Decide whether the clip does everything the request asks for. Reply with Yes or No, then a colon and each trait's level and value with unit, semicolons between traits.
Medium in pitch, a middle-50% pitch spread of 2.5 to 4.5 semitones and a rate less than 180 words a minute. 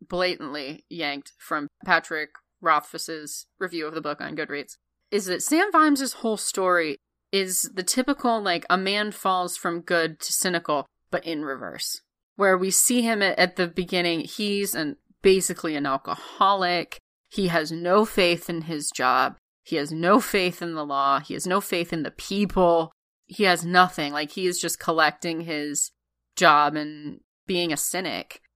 Yes: medium, 175 Hz; average, 3.8 semitones; average, 165 wpm